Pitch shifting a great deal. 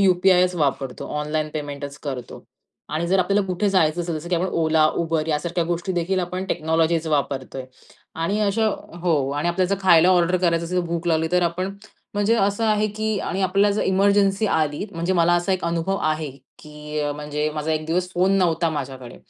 No: average, 3.3 semitones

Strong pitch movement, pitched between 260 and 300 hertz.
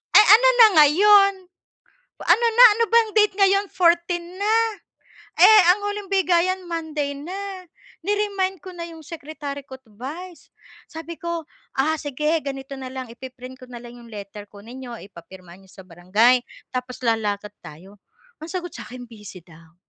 Yes: wide, 8.1 semitones; very high, 290 Hz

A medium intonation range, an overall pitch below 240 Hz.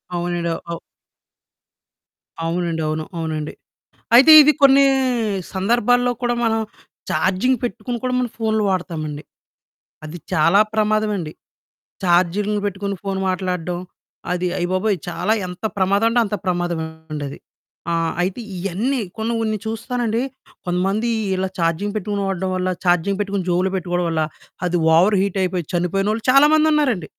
Yes: average, 3.9 semitones; high, 190 Hz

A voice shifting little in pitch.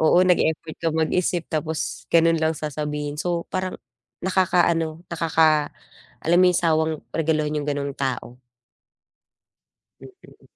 Yes: narrow, 1.9 semitones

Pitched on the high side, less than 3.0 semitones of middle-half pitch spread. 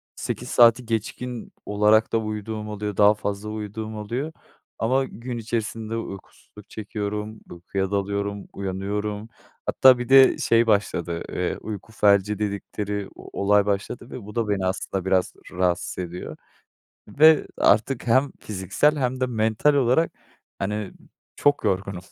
No: low, 105 Hz; narrow, 2.5 semitones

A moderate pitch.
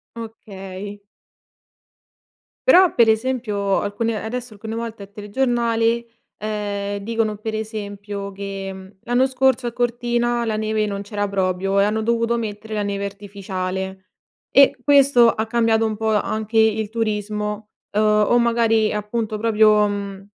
No: high, 215 Hz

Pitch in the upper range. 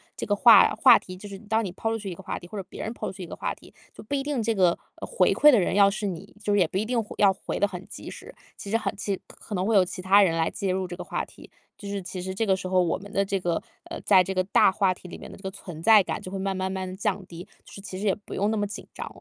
Yes: high, 195 Hz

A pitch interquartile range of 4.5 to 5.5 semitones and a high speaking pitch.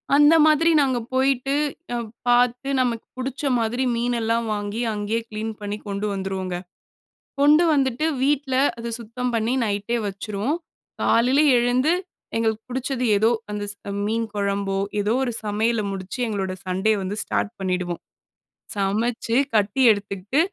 No: average, 3.8 semitones; high, 230 Hz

